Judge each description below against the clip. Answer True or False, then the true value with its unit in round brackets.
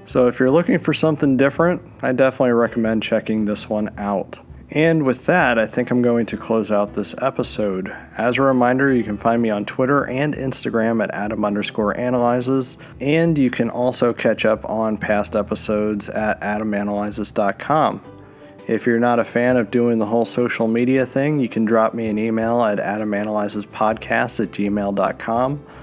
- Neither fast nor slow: True (170 wpm)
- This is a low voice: True (115 Hz)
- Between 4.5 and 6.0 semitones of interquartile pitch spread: False (3.5 semitones)